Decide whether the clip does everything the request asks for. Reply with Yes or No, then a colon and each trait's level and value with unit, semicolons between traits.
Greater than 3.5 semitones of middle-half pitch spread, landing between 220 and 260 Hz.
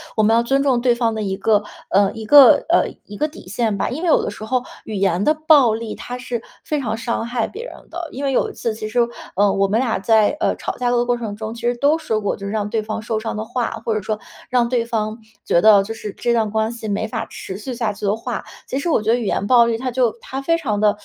No: narrow, 2.6 semitones; high, 225 Hz